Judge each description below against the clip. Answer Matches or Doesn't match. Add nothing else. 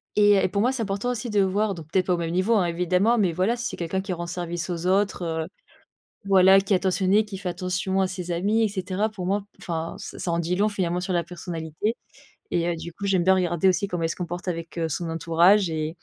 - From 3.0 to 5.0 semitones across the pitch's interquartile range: Doesn't match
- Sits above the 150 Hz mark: Matches